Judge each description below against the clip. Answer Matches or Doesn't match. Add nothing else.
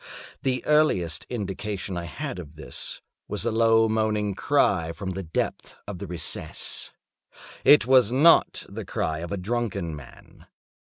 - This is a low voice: Matches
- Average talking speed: Matches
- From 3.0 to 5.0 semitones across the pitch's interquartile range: Doesn't match